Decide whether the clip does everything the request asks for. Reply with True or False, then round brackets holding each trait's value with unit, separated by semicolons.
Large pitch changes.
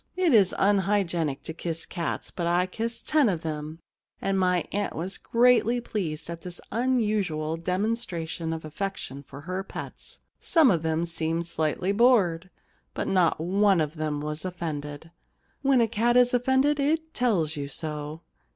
True (6.0 semitones)